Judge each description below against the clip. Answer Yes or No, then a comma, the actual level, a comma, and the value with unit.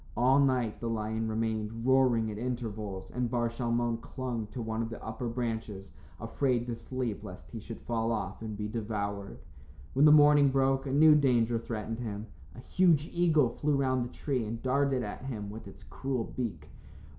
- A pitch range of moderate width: Yes, average, 3.0 semitones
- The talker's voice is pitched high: No, low, 115 Hz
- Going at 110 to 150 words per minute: No, average, 180 wpm